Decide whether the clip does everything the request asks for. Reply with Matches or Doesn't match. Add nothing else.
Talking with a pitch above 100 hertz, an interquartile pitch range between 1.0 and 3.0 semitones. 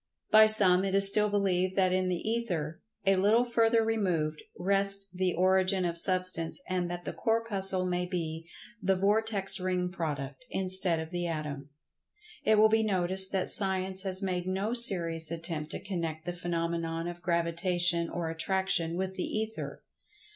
Matches